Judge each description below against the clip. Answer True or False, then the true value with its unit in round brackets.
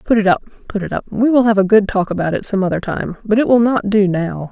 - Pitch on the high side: True (205 Hz)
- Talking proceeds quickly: True (305 wpm)